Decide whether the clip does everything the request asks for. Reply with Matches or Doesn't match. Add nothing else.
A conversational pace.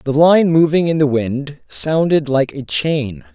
Matches